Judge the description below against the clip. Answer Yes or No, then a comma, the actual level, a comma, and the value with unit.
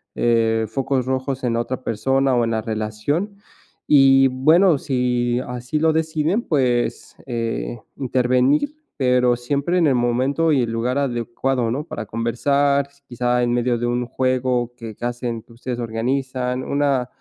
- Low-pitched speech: Yes, low, 125 Hz